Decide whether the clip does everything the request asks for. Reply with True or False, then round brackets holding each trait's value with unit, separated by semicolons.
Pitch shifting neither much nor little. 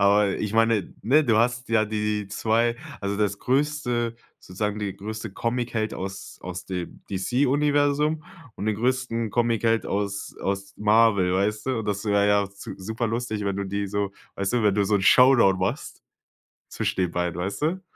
True (3.1 semitones)